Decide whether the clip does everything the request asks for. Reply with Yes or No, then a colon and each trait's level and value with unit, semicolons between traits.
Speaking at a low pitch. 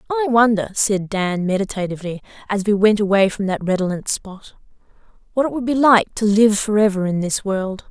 No: high, 205 Hz